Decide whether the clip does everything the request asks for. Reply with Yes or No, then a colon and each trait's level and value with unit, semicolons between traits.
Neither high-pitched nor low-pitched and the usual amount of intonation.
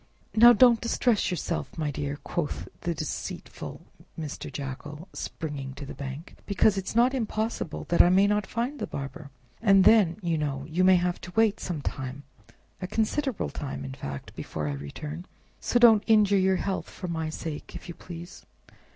No: medium, 175 Hz; wide, 6.2 semitones